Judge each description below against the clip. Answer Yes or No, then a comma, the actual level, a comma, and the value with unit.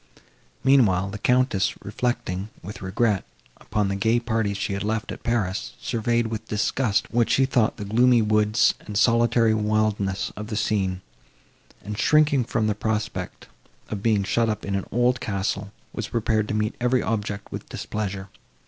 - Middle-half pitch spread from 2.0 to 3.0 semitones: Yes, narrow, 2.6 semitones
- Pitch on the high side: No, low, 110 Hz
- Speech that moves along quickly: No, average, 165 wpm